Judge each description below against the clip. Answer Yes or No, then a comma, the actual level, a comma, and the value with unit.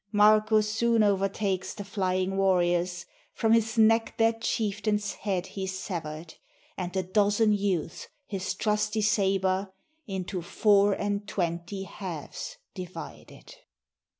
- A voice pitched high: Yes, high, 200 Hz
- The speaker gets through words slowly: Yes, slow, 115 wpm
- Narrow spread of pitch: Yes, narrow, 2.3 semitones